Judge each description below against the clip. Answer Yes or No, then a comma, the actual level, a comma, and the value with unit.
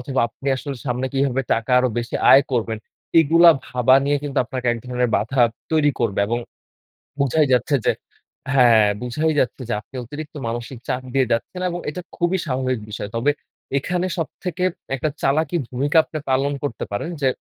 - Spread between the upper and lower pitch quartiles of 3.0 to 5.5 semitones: Yes, average, 3.5 semitones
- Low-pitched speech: Yes, low, 130 Hz